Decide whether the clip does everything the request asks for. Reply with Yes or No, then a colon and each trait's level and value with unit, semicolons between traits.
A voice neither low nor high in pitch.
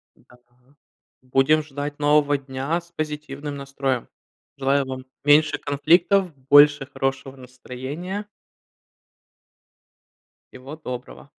Yes: medium, 145 Hz